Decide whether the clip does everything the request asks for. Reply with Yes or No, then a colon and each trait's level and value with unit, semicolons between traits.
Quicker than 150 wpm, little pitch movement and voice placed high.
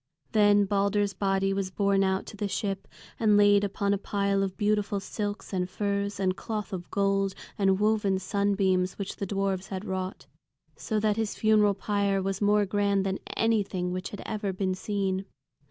Yes: average, 175 wpm; narrow, 1.2 semitones; high, 200 Hz